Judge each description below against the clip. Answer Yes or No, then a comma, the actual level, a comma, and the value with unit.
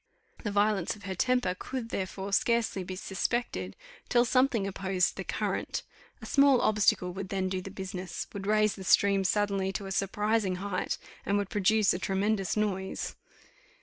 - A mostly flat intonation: Yes, narrow, 2.0 semitones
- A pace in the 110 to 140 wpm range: No, average, 165 wpm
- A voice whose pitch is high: Yes, high, 195 Hz